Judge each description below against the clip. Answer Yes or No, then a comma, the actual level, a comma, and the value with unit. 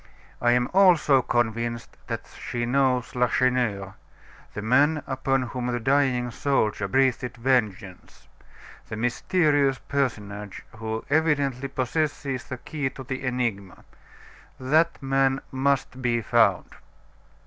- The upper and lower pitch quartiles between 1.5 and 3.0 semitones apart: Yes, narrow, 2.5 semitones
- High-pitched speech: No, low, 125 Hz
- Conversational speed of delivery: No, slow, 115 wpm